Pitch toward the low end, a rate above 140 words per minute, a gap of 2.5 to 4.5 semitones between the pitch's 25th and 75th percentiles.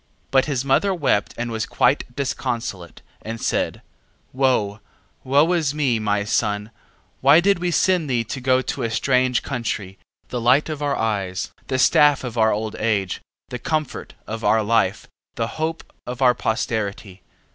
Yes: low, 125 Hz; average, 170 wpm; average, 4.2 semitones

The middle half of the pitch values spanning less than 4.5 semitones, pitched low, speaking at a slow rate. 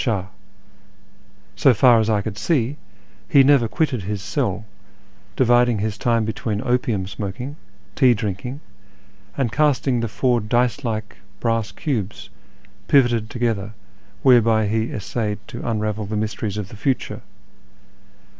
Yes: average, 2.9 semitones; low, 115 Hz; slow, 125 wpm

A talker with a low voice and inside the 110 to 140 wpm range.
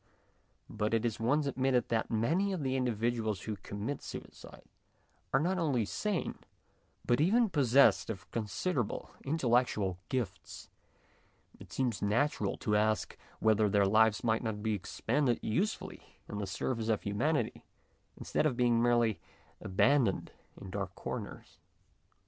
Yes: low, 115 Hz; slow, 135 wpm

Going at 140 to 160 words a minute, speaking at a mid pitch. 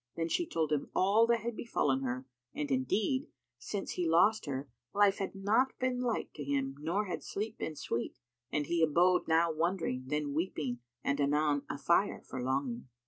No: average, 180 wpm; medium, 160 Hz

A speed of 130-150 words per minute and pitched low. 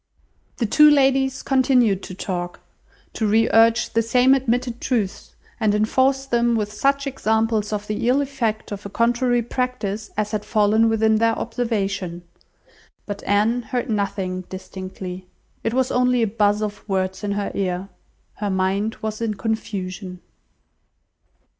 No: average, 145 wpm; high, 220 Hz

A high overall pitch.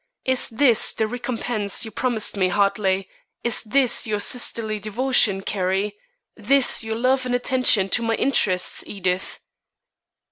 Yes: high, 220 Hz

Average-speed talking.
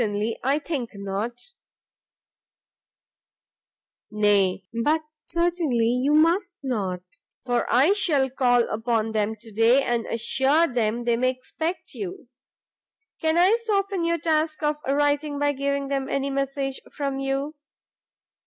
No: slow, 125 wpm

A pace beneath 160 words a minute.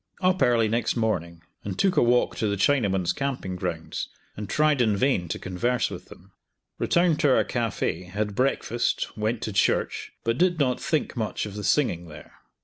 No: average, 185 wpm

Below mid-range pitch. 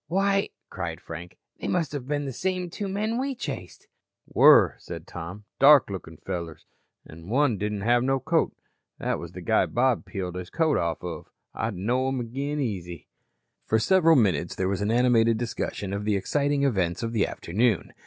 Yes: low, 115 Hz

